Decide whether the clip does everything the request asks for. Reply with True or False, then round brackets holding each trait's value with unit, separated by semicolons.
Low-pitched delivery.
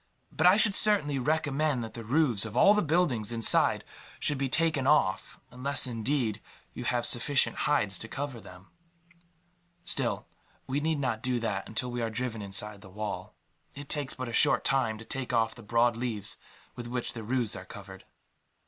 True (125 Hz)